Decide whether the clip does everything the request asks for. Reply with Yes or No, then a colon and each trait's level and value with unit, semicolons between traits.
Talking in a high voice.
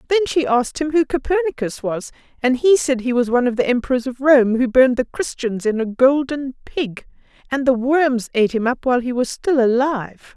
Yes: very high, 260 Hz